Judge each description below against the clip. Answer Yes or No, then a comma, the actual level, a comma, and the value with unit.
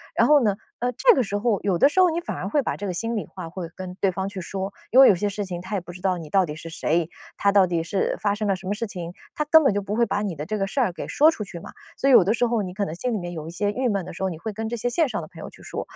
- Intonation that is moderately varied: Yes, average, 4.3 semitones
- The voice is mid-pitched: No, high, 200 Hz